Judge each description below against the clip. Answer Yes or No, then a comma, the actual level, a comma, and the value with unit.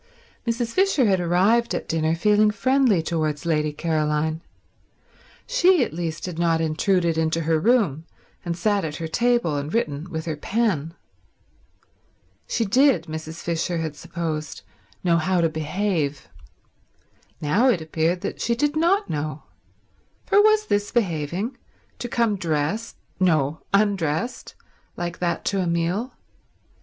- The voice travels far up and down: Yes, wide, 5.8 semitones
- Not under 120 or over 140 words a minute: Yes, slow, 135 wpm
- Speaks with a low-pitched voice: No, medium, 170 Hz